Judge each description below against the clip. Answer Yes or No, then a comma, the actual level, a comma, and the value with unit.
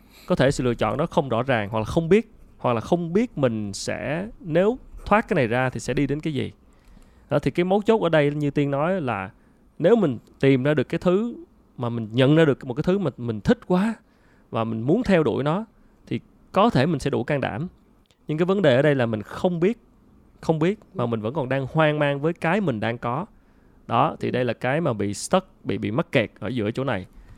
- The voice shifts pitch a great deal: Yes, wide, 7.1 semitones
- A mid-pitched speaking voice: Yes, medium, 150 Hz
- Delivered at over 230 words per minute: Yes, fast, 250 wpm